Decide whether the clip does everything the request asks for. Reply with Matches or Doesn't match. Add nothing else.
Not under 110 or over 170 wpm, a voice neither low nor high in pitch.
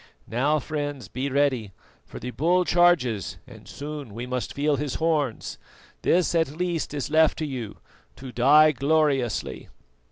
Matches